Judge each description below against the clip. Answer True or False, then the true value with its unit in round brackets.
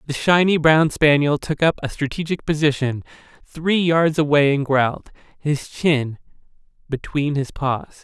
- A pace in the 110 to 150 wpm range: True (140 wpm)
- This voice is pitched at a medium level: True (150 Hz)